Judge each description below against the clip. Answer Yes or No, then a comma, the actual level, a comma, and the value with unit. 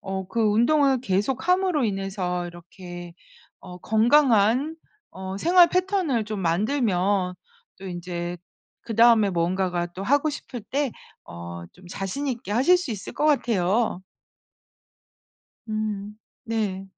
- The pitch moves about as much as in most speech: No, wide, 6.2 semitones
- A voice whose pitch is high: Yes, high, 210 Hz